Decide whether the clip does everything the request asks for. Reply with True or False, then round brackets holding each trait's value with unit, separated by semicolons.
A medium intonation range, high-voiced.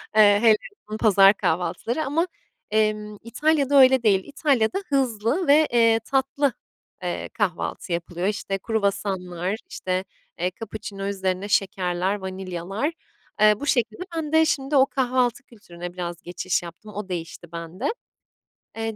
False (5.8 semitones; 210 Hz)